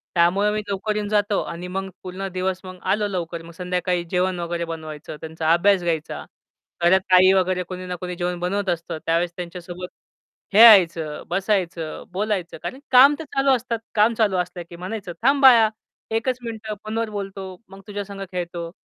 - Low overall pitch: No, medium, 185 Hz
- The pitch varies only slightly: No, average, 3.1 semitones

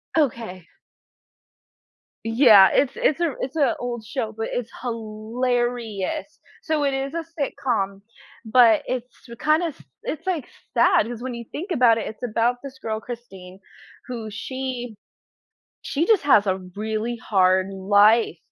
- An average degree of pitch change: Yes, average, 3.6 semitones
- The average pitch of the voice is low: No, high, 235 Hz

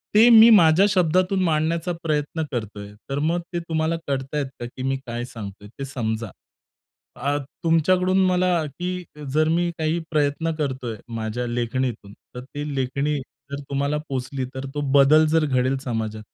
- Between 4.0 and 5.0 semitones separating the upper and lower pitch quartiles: Yes, average, 4.3 semitones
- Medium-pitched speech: Yes, medium, 145 Hz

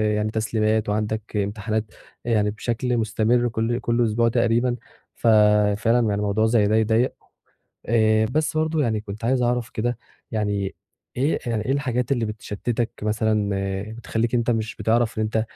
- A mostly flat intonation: Yes, narrow, 1.9 semitones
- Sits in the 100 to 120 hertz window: Yes, low, 110 Hz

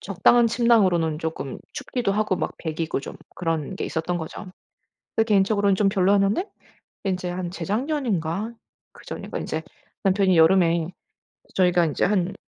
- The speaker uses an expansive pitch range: No, average, 3.7 semitones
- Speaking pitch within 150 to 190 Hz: Yes, medium, 185 Hz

